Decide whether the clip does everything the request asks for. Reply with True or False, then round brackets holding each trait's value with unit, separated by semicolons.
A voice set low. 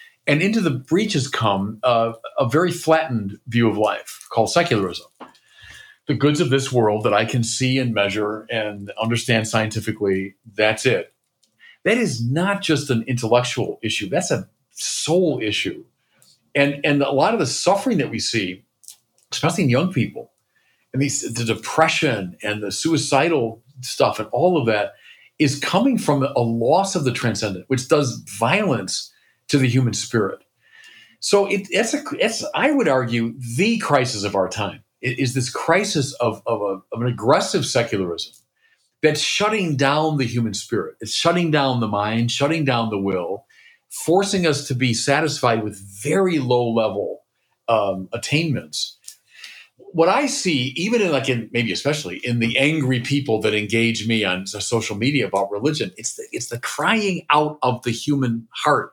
True (130 Hz)